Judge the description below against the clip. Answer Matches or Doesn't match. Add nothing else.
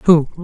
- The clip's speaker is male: Doesn't match